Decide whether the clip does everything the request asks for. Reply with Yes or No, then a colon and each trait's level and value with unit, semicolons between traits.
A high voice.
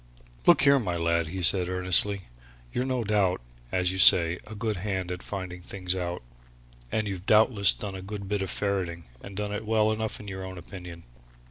No: very low, 95 Hz